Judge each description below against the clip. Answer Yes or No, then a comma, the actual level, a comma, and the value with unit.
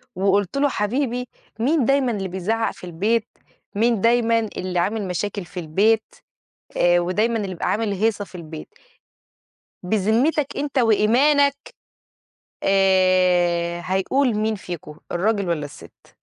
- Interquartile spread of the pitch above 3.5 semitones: Yes, average, 4.2 semitones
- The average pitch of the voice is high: Yes, high, 205 Hz